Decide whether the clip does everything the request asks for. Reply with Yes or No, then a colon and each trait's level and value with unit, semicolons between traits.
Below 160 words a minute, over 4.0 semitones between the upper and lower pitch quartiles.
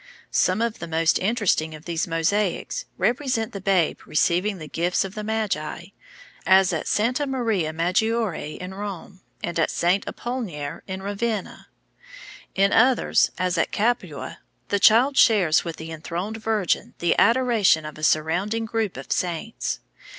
Yes: average, 150 wpm; average, 4.9 semitones